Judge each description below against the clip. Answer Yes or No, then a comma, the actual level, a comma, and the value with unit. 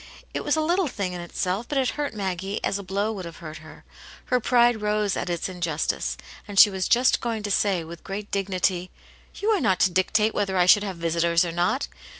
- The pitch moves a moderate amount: Yes, average, 3.7 semitones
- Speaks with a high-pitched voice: Yes, high, 195 Hz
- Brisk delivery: Yes, fast, 225 wpm